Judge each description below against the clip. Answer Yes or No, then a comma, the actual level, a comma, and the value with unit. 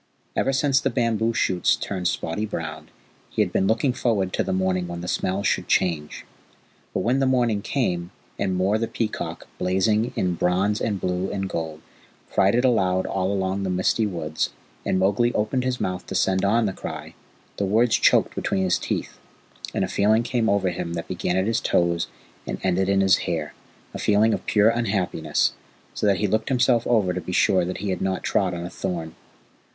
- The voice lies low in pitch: Yes, very low, 95 Hz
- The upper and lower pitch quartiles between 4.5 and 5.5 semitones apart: No, average, 3.5 semitones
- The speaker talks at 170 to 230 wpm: Yes, average, 200 wpm